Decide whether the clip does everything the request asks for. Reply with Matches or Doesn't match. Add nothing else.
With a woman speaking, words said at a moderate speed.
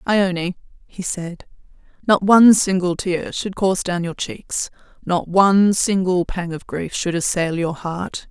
Matches